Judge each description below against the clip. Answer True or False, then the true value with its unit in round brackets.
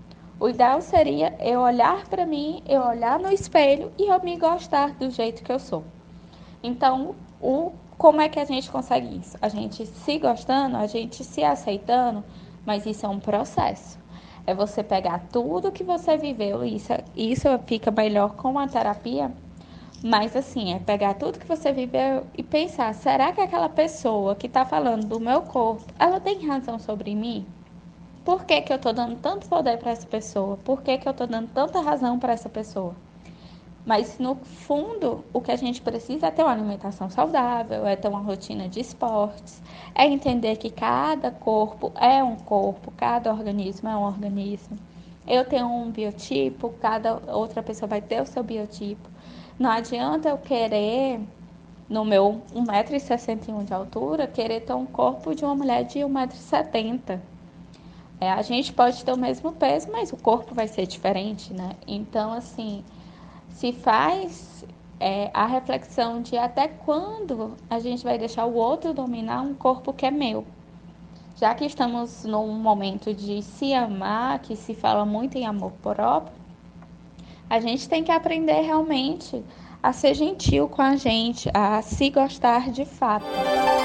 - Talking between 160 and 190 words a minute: True (170 wpm)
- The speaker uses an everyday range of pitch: True (4.5 semitones)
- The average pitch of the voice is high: True (235 Hz)